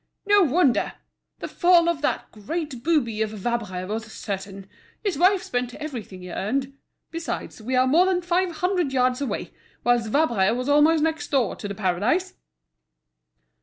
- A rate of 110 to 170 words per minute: Yes, average, 165 wpm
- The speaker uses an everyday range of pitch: No, wide, 7.3 semitones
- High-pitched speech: Yes, very high, 260 Hz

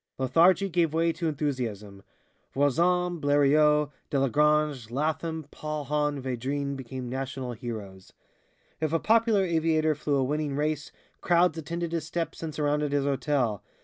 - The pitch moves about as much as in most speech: Yes, average, 3.2 semitones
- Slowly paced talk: Yes, slow, 130 wpm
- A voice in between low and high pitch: Yes, medium, 150 Hz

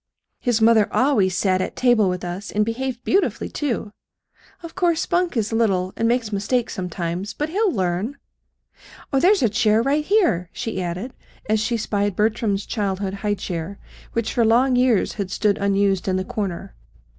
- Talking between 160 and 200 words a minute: Yes, average, 170 wpm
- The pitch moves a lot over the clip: No, average, 4.2 semitones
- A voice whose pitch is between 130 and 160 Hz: No, high, 215 Hz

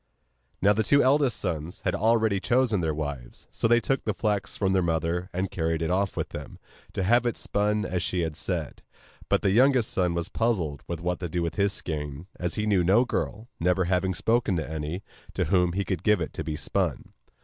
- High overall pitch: No, very low, 95 Hz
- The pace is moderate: No, fast, 215 wpm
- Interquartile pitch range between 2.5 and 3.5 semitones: No, average, 4.1 semitones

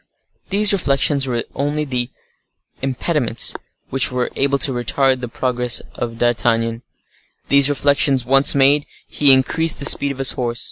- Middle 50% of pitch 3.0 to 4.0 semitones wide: No, narrow, 2.5 semitones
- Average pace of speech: Yes, average, 145 wpm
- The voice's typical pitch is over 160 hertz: No, low, 135 Hz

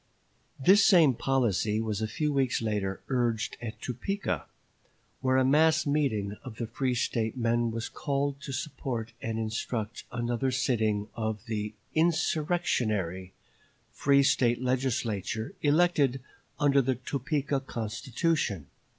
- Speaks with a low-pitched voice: Yes, low, 125 Hz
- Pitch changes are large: No, average, 4.1 semitones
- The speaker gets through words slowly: Yes, slow, 125 wpm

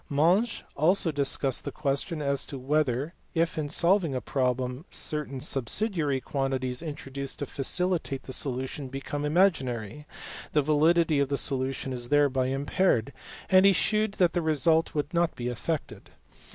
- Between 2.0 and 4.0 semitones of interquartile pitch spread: Yes, average, 3.7 semitones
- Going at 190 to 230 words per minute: No, average, 150 wpm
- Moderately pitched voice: Yes, medium, 145 Hz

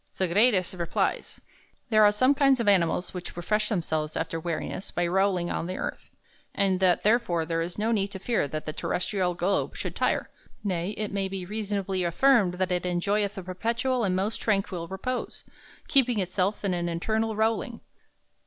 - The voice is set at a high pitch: Yes, high, 195 Hz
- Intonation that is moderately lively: Yes, average, 3.4 semitones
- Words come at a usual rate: Yes, average, 175 wpm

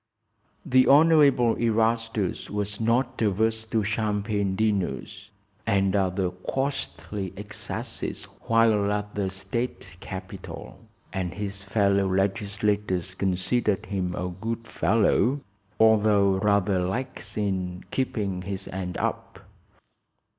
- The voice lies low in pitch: Yes, low, 105 Hz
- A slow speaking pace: Yes, slow, 105 wpm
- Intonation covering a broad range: No, average, 2.8 semitones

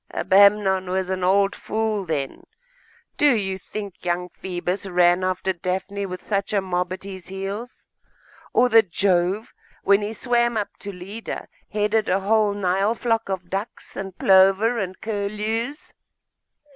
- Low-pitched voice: No, high, 195 Hz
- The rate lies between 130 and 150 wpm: Yes, average, 145 wpm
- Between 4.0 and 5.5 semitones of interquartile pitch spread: No, narrow, 2.4 semitones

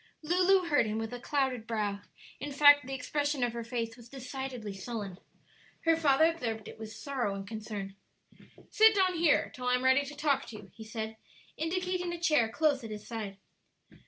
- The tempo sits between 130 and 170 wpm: No, average, 190 wpm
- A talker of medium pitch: No, very high, 255 Hz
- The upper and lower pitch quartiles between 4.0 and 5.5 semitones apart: Yes, average, 5.2 semitones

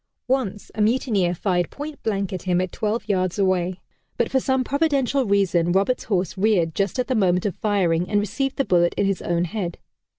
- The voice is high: Yes, high, 200 Hz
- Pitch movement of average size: Yes, average, 4.6 semitones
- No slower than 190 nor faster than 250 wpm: Yes, average, 200 wpm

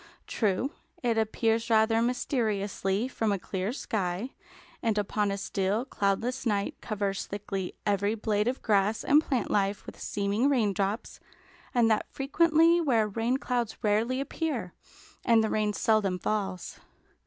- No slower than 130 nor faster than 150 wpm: Yes, average, 140 wpm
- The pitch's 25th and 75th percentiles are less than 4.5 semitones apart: Yes, average, 3.3 semitones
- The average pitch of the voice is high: Yes, high, 215 Hz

